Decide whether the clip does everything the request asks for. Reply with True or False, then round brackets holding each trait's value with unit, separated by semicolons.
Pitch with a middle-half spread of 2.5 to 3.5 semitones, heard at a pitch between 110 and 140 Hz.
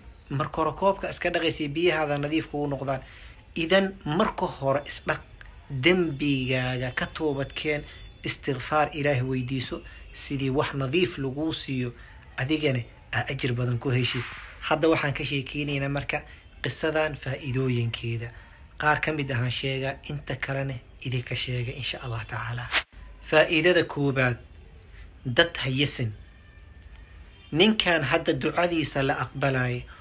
False (3.9 semitones; 135 Hz)